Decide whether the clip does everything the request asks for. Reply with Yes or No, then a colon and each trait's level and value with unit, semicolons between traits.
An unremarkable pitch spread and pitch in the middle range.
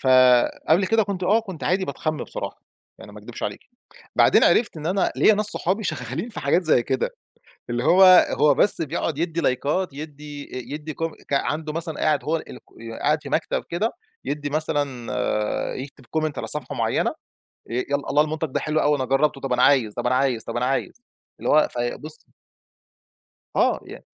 Yes: average, 3.6 semitones; medium, 150 Hz